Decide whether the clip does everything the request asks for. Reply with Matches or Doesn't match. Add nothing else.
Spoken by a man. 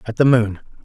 Matches